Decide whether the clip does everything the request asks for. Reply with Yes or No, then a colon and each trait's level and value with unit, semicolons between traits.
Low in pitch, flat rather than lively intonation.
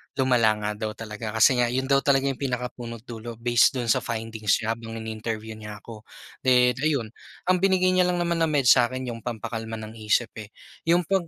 No: low, 120 Hz; average, 3.5 semitones